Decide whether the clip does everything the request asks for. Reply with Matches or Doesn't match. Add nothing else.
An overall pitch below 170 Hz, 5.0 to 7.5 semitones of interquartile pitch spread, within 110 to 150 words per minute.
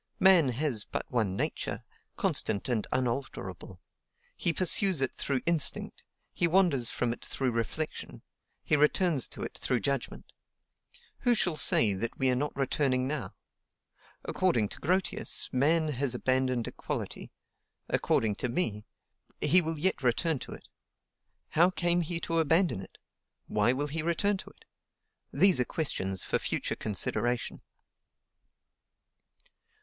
Matches